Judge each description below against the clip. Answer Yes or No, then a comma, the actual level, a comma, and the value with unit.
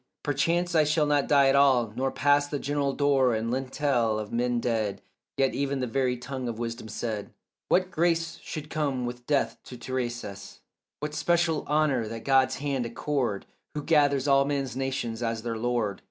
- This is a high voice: No, low, 135 Hz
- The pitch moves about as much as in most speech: Yes, average, 3.4 semitones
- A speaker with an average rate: Yes, average, 180 wpm